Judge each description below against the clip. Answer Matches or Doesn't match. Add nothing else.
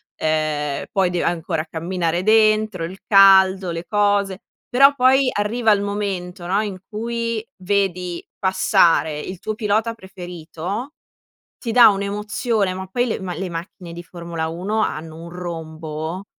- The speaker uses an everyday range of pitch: Matches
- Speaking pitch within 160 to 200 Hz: Matches